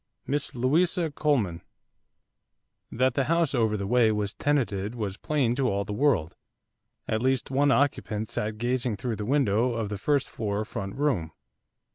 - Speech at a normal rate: Yes, average, 160 wpm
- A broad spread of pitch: No, average, 5.0 semitones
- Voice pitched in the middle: No, low, 120 Hz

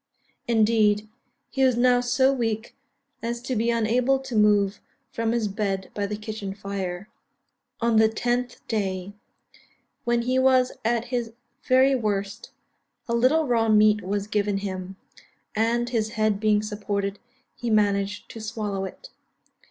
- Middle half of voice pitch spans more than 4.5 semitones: No, average, 2.7 semitones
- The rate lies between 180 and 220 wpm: No, average, 145 wpm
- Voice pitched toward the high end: Yes, high, 220 Hz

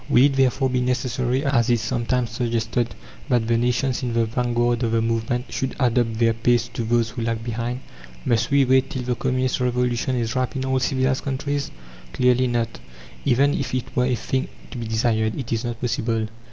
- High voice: No, low, 120 Hz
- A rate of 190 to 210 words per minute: Yes, average, 200 wpm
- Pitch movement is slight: Yes, narrow, 1.9 semitones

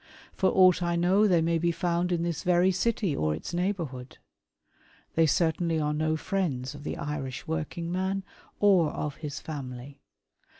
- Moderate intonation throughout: Yes, average, 3.5 semitones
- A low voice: No, medium, 170 Hz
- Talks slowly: No, average, 165 wpm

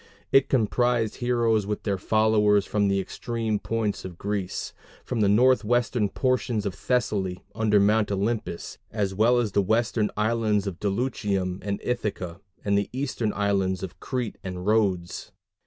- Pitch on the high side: No, low, 105 Hz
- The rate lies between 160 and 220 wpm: No, average, 150 wpm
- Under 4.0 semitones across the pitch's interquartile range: Yes, average, 2.8 semitones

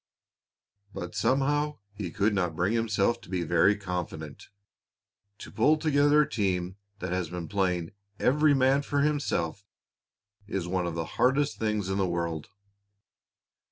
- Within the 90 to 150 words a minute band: Yes, average, 145 wpm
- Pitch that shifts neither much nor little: No, wide, 7.4 semitones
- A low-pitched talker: Yes, low, 100 Hz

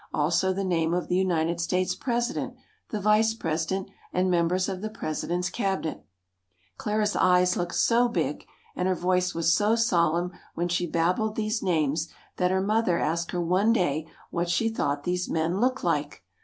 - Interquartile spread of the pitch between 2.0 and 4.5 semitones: Yes, average, 3.6 semitones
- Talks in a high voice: No, medium, 180 Hz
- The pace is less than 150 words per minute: No, average, 170 wpm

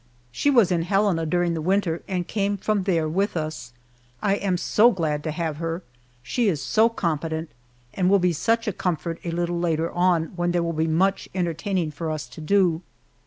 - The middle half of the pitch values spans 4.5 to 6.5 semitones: No, average, 3.2 semitones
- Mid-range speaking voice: Yes, medium, 175 Hz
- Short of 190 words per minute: No, average, 200 wpm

